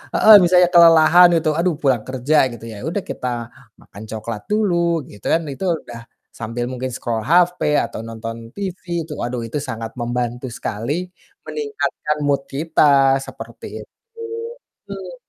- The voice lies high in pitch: No, low, 135 Hz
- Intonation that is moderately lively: No, wide, 6.7 semitones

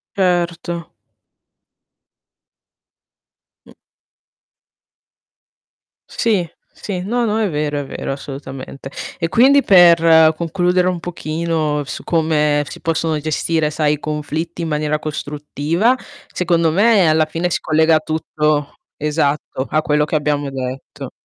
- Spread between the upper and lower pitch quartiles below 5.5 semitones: Yes, narrow, 2.5 semitones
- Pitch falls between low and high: Yes, medium, 160 Hz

